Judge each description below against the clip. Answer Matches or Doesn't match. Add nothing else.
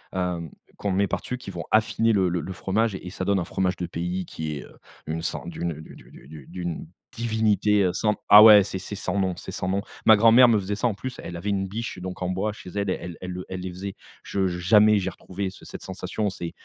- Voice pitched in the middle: Doesn't match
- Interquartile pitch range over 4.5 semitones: Doesn't match